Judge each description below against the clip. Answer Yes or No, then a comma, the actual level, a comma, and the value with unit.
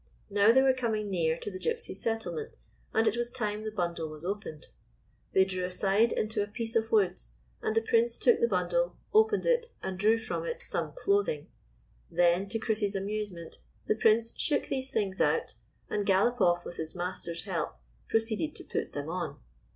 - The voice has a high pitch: Yes, high, 215 Hz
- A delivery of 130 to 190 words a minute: Yes, average, 180 wpm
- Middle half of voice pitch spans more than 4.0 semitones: Yes, average, 4.4 semitones